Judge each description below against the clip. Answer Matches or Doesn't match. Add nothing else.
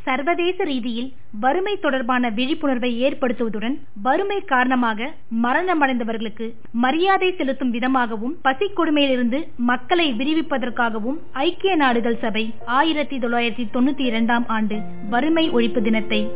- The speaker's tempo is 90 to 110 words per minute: Matches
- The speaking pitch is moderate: Doesn't match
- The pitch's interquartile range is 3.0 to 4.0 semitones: Matches